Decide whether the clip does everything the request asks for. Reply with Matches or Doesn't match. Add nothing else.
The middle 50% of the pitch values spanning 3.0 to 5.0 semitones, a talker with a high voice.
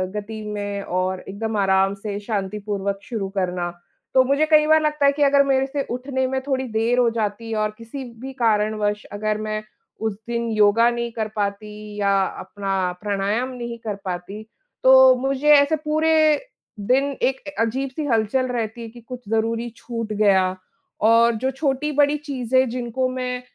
Matches